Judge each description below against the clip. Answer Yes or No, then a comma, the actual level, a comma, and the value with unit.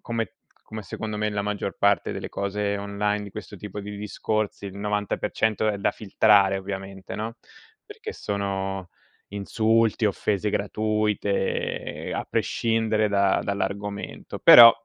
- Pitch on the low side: Yes, low, 105 Hz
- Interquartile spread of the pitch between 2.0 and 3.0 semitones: No, narrow, 1.3 semitones